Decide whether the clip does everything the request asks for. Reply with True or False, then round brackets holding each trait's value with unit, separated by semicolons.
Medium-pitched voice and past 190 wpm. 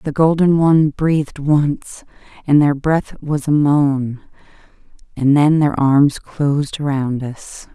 False (145 Hz; 140 wpm)